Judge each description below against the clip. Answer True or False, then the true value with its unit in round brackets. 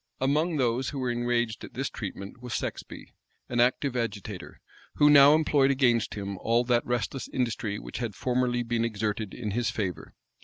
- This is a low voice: True (120 Hz)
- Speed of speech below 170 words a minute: False (175 wpm)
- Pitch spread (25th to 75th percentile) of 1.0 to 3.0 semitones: True (2.7 semitones)